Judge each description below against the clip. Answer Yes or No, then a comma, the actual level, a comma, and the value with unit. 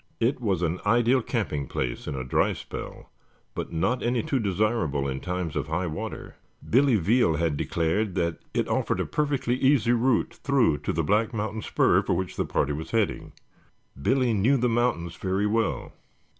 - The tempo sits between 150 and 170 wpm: No, average, 180 wpm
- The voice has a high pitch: No, low, 105 Hz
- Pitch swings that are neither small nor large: No, wide, 6.4 semitones